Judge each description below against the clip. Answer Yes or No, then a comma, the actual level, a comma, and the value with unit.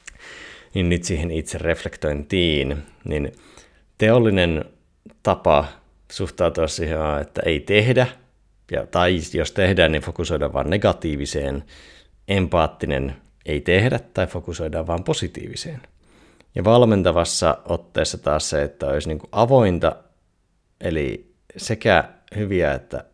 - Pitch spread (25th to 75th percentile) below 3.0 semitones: No, average, 4.0 semitones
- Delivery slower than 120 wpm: Yes, average, 100 wpm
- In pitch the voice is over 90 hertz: No, very low, 85 Hz